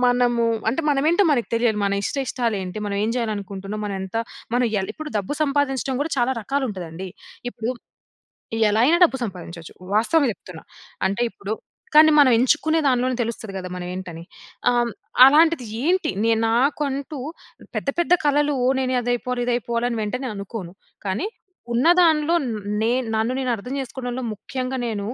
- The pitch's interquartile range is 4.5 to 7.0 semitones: Yes, average, 4.9 semitones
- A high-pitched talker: Yes, high, 245 Hz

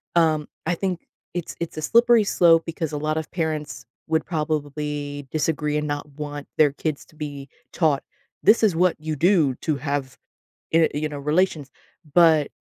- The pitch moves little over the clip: Yes, narrow, 2.2 semitones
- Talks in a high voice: No, medium, 155 Hz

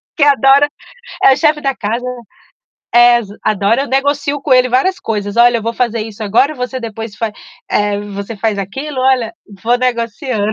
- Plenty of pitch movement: No, average, 3.8 semitones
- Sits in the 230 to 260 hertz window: Yes, high, 240 Hz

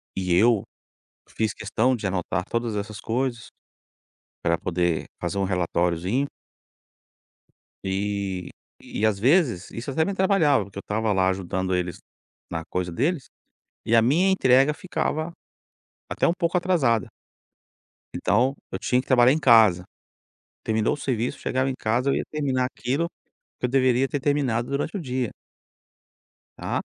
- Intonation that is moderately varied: No, wide, 5.9 semitones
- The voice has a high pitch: No, low, 120 Hz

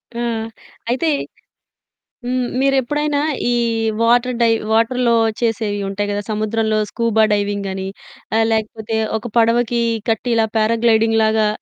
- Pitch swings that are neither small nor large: No, narrow, 1.9 semitones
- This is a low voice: No, high, 225 Hz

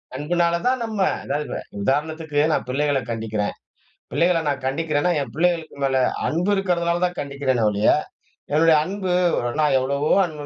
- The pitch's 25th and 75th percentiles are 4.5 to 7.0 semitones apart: No, average, 4.0 semitones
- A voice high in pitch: No, medium, 150 Hz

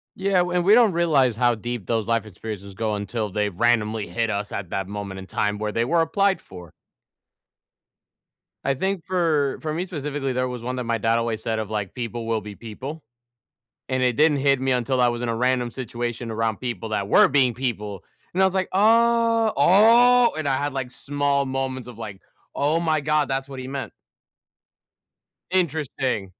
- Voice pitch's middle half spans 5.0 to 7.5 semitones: Yes, wide, 5.5 semitones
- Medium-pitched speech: No, low, 125 Hz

